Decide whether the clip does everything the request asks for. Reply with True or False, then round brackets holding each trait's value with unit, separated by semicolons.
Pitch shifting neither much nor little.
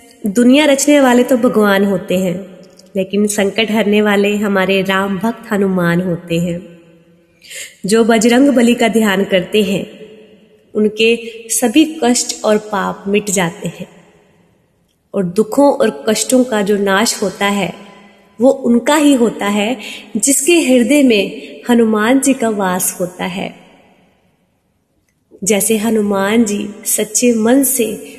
True (3.4 semitones)